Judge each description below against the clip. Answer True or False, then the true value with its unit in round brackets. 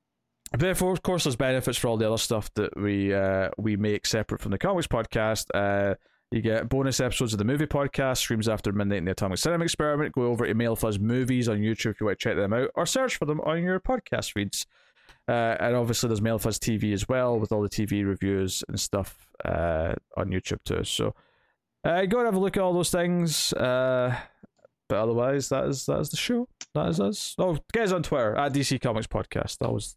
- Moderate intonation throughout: False (6.0 semitones)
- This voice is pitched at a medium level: False (120 Hz)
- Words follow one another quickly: True (225 wpm)